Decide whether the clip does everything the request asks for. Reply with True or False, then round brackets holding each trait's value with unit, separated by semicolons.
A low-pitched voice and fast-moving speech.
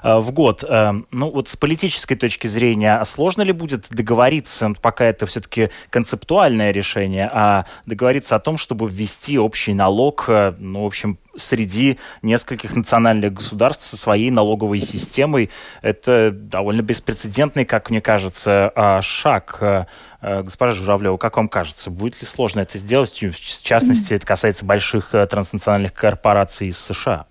False (110 Hz; 140 wpm)